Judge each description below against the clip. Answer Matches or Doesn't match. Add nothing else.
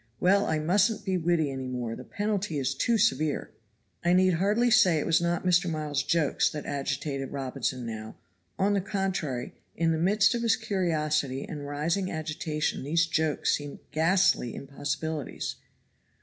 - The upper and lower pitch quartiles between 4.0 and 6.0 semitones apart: Matches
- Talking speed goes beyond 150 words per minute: Matches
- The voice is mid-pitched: Matches